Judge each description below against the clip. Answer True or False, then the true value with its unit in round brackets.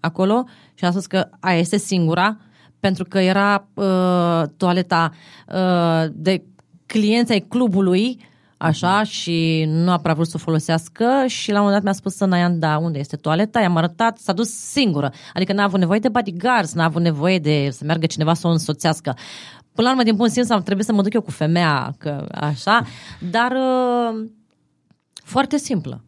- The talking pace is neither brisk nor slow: False (185 wpm)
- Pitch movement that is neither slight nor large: True (4.8 semitones)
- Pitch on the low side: False (185 Hz)